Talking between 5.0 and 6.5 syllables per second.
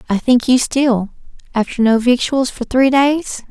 No: 4.2 syllables/s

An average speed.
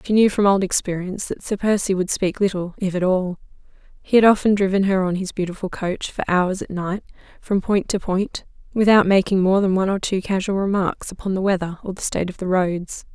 No: fast, 225 wpm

